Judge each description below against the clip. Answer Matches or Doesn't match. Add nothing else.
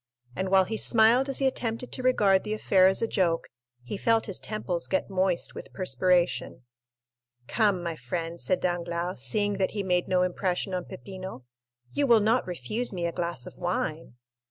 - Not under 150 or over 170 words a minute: Doesn't match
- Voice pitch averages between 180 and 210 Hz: Matches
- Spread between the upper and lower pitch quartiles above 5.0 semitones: Doesn't match